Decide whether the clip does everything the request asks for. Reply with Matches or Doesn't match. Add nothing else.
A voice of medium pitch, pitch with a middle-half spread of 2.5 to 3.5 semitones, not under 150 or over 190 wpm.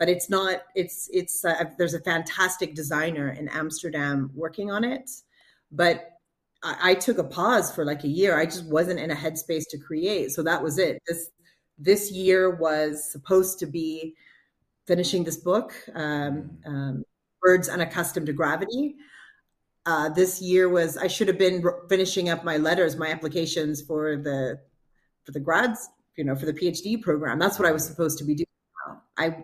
Matches